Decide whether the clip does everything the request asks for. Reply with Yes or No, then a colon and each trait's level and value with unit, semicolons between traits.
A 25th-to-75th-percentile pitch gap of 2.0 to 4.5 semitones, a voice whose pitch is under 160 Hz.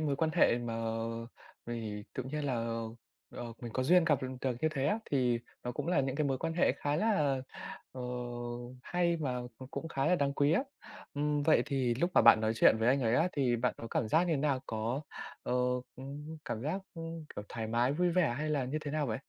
Yes: average, 4.1 semitones; medium, 140 Hz